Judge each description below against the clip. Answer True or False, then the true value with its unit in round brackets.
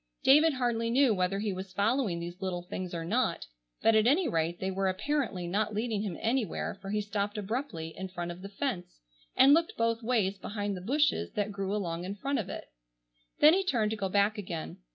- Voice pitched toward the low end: False (205 Hz)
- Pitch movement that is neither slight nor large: True (4.2 semitones)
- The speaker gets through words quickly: True (215 wpm)